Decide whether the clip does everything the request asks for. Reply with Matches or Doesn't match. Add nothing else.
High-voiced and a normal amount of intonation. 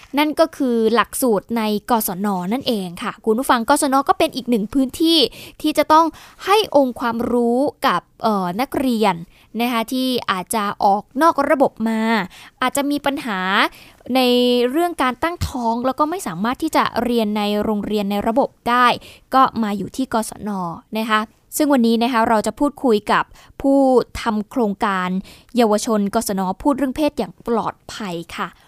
Matches